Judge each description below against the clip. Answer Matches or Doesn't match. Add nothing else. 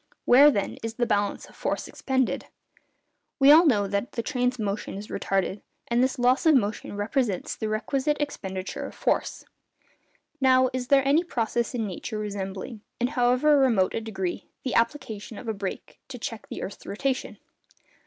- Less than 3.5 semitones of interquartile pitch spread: Doesn't match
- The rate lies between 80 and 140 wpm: Doesn't match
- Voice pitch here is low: Doesn't match